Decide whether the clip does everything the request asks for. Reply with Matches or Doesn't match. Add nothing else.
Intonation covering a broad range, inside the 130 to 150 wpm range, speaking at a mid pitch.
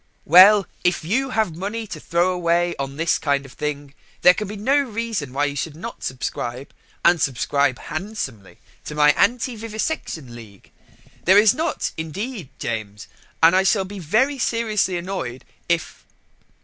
Doesn't match